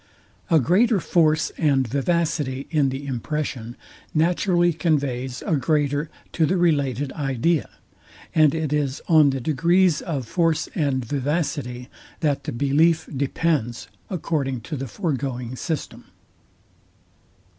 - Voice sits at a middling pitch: Yes, medium, 145 Hz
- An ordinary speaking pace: No, slow, 120 wpm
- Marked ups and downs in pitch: No, average, 3.6 semitones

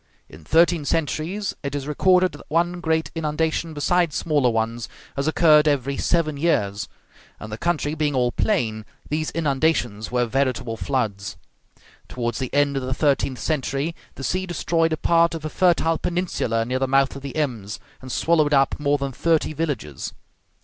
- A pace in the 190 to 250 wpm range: No, average, 170 wpm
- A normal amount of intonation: Yes, average, 4.3 semitones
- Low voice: No, medium, 145 Hz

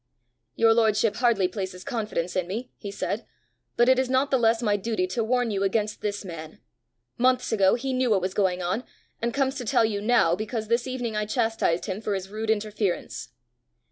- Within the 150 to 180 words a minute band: No, fast, 205 wpm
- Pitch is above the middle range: Yes, high, 215 Hz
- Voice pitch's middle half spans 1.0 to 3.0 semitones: No, average, 3.6 semitones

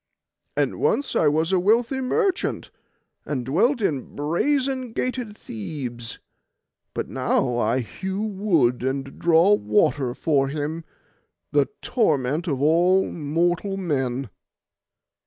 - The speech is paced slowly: Yes, slow, 115 wpm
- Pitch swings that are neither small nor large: No, wide, 7.3 semitones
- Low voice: No, medium, 165 Hz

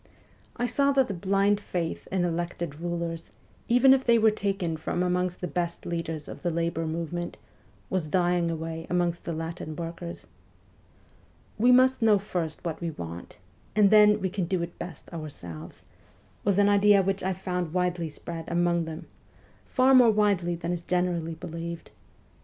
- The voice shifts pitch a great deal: No, average, 3.1 semitones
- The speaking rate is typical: Yes, average, 170 wpm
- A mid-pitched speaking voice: Yes, medium, 175 Hz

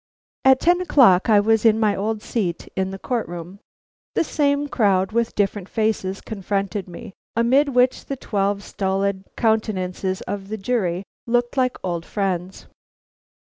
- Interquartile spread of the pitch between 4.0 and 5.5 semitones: No, average, 3.6 semitones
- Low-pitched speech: No, high, 205 Hz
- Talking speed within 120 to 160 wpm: Yes, average, 150 wpm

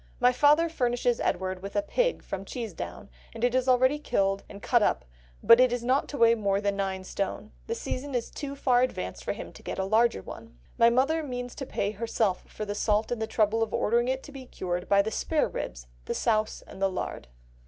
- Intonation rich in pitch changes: No, average, 4.3 semitones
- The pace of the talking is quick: Yes, fast, 220 wpm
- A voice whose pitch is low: No, high, 230 Hz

